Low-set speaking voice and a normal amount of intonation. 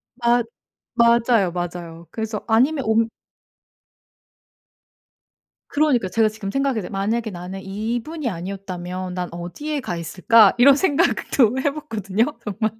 No: high, 220 Hz; average, 4.6 semitones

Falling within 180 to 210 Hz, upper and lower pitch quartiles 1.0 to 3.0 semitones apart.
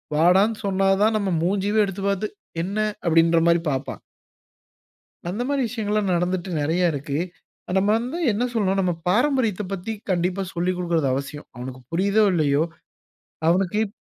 No: medium, 185 Hz; average, 3.6 semitones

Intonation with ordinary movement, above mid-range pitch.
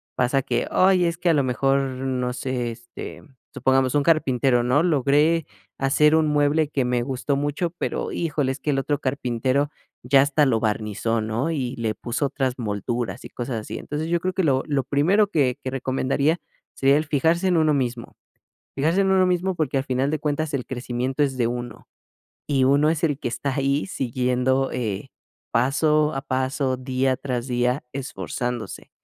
No: average, 3.1 semitones; low, 135 Hz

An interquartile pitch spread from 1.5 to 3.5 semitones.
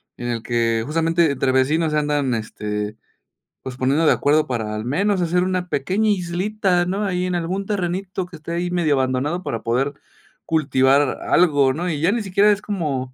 No: wide, 5.5 semitones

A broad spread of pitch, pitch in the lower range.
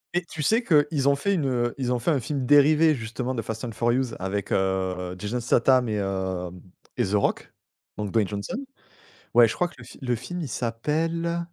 Yes: wide, 6.2 semitones; low, 120 Hz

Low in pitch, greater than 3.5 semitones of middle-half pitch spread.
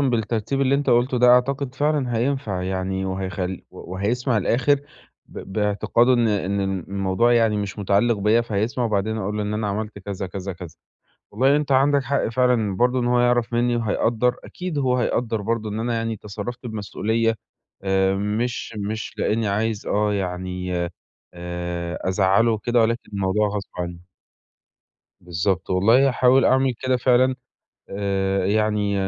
Yes: low, 110 Hz; average, 3.9 semitones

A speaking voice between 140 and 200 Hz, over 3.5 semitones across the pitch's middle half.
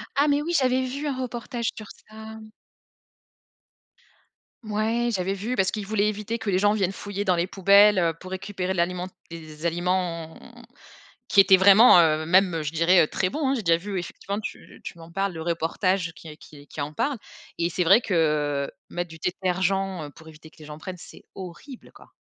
Yes: medium, 185 Hz; average, 4.0 semitones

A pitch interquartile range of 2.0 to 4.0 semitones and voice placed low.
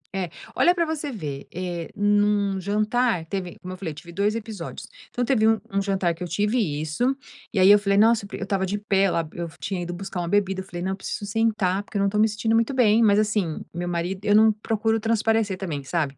No: average, 3.3 semitones; high, 200 Hz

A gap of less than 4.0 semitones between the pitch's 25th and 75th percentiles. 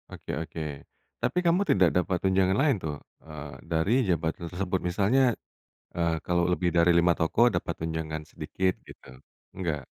Yes: average, 2.7 semitones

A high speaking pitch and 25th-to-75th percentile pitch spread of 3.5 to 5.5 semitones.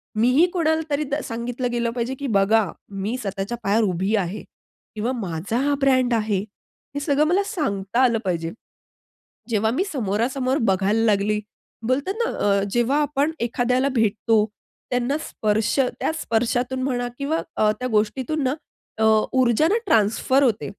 Yes: high, 240 Hz; average, 4.1 semitones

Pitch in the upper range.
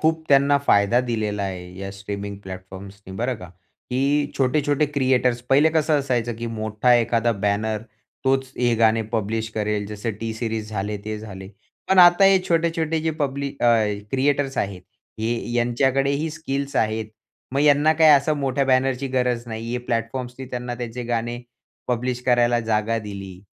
No: low, 120 Hz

